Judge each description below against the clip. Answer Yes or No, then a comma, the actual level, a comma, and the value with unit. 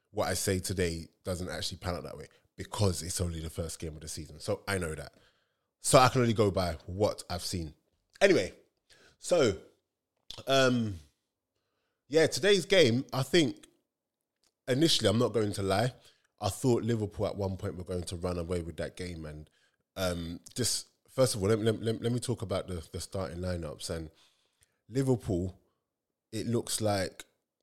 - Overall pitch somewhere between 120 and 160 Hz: No, very low, 95 Hz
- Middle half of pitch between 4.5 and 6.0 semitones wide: Yes, average, 4.8 semitones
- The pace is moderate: Yes, average, 180 wpm